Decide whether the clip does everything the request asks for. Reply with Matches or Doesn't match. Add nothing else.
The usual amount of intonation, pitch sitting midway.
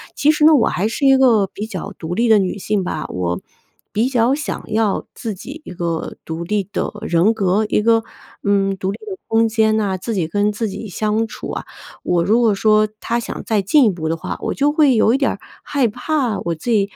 Doesn't match